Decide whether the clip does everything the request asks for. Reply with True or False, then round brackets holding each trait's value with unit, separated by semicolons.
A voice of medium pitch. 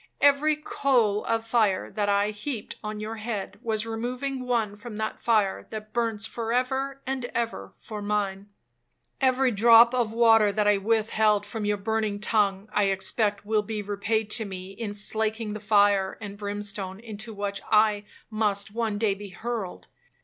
False (215 Hz)